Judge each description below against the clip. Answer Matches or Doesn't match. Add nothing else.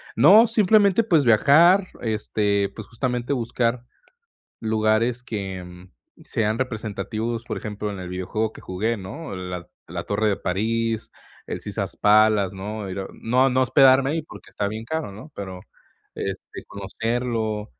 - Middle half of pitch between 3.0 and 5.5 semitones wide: Matches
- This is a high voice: Doesn't match